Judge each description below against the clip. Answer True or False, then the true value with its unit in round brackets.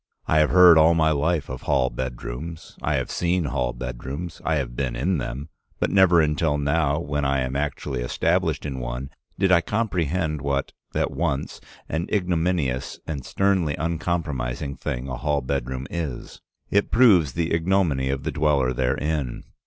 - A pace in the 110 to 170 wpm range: True (165 wpm)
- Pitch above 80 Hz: False (75 Hz)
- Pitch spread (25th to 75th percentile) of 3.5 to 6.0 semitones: True (4.2 semitones)